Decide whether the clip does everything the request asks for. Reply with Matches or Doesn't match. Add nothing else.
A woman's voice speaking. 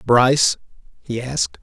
Doesn't match